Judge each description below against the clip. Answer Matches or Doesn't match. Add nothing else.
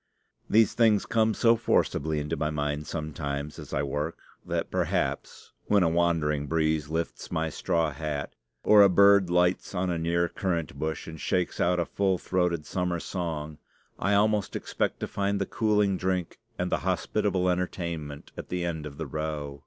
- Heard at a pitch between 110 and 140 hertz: Doesn't match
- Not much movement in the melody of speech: Doesn't match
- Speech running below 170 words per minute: Doesn't match